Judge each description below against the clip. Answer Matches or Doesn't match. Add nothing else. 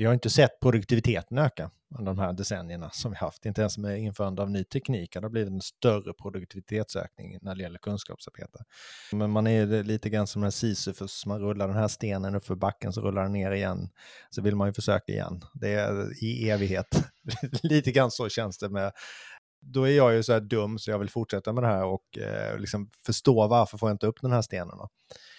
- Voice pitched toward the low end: Matches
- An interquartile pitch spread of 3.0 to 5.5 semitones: Doesn't match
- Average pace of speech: Doesn't match